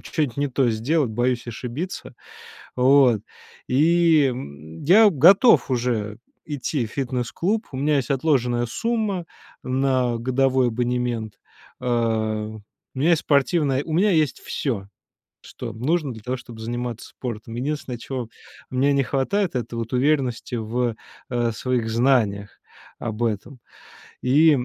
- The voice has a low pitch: Yes, low, 125 Hz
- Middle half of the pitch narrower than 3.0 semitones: No, average, 3.6 semitones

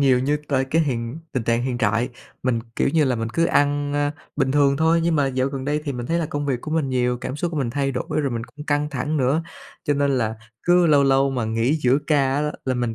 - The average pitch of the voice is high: No, low, 135 Hz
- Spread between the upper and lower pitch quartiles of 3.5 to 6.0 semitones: No, average, 2.9 semitones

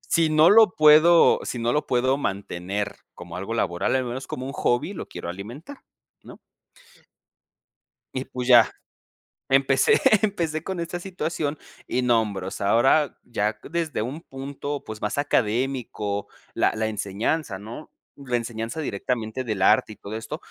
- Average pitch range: No, wide, 5.8 semitones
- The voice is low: Yes, low, 125 Hz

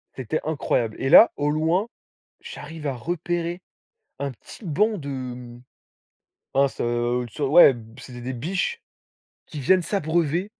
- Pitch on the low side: No, medium, 150 Hz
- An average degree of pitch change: Yes, average, 4.8 semitones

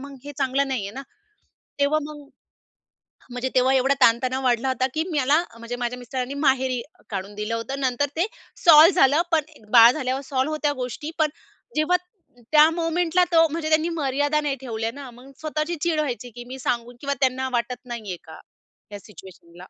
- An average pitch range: Yes, average, 3.8 semitones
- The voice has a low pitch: No, very high, 265 Hz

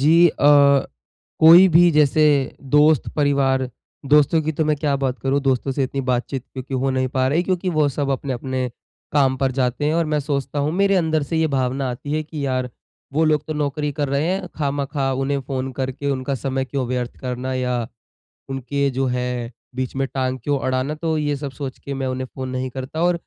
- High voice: No, medium, 140 Hz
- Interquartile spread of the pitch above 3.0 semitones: No, narrow, 2.5 semitones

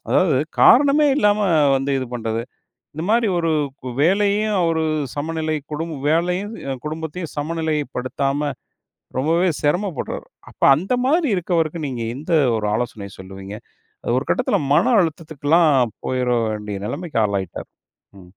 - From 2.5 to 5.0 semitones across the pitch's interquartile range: No, wide, 5.6 semitones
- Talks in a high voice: No, medium, 155 Hz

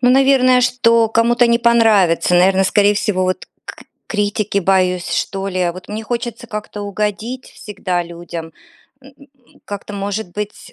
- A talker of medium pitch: No, high, 205 Hz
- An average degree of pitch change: Yes, average, 4.0 semitones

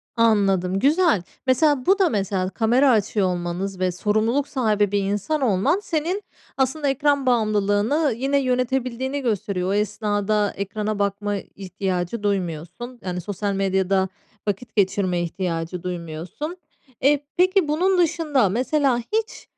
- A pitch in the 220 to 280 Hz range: No, high, 210 Hz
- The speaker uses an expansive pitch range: Yes, wide, 6.0 semitones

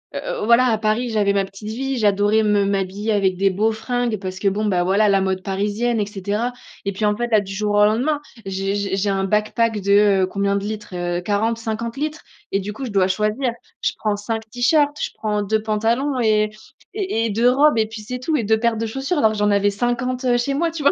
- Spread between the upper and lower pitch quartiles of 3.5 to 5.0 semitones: No, average, 3.0 semitones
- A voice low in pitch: No, high, 215 Hz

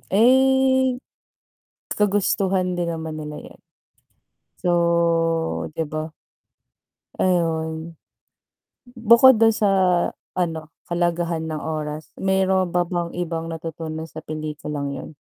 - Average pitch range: Yes, average, 3.0 semitones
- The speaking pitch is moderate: Yes, medium, 170 Hz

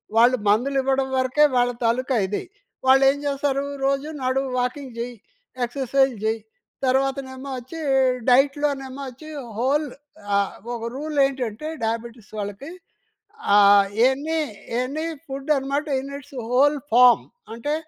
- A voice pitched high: Yes, very high, 265 Hz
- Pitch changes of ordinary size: No, narrow, 2.3 semitones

